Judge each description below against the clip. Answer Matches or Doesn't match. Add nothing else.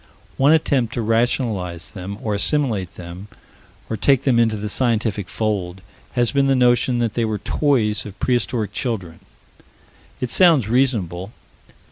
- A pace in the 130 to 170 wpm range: Matches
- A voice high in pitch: Doesn't match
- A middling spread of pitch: Matches